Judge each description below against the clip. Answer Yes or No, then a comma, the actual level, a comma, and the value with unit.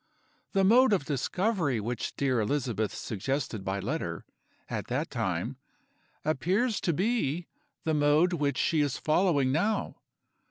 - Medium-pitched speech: Yes, medium, 150 Hz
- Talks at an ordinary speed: No, slow, 130 wpm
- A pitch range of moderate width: No, wide, 6.1 semitones